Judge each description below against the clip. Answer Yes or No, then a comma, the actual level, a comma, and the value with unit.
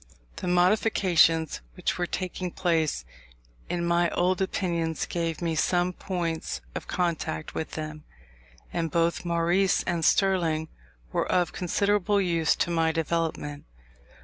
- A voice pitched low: No, medium, 170 Hz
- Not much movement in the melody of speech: Yes, narrow, 1.9 semitones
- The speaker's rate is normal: No, slow, 125 wpm